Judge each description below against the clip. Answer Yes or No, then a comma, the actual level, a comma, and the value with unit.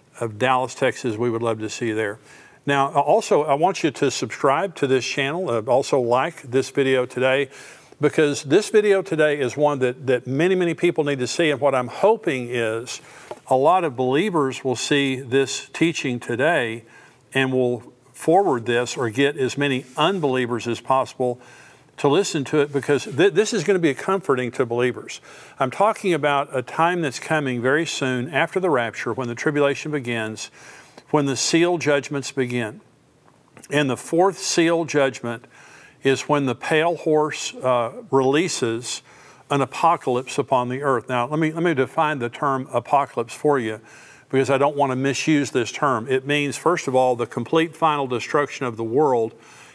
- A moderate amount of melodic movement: Yes, average, 3.5 semitones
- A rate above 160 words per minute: Yes, average, 175 wpm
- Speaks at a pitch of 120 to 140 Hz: Yes, low, 135 Hz